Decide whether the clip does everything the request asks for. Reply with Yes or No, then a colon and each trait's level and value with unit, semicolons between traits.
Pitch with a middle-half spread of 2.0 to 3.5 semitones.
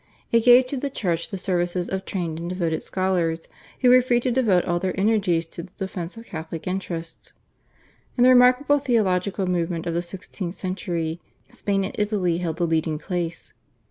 No: average, 3.9 semitones